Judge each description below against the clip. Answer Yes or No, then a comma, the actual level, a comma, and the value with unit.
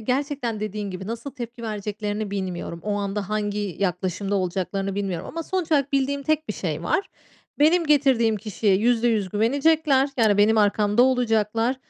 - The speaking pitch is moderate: No, high, 215 Hz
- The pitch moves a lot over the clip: No, average, 4.7 semitones